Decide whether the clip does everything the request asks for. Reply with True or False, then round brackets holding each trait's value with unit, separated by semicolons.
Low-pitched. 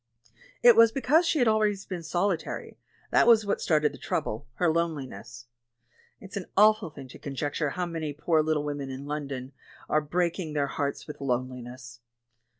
False (155 Hz)